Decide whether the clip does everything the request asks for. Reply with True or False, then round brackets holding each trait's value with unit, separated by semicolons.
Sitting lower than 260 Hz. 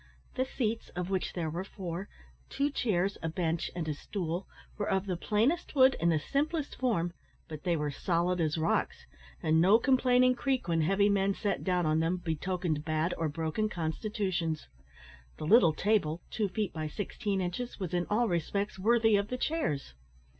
True (185 Hz)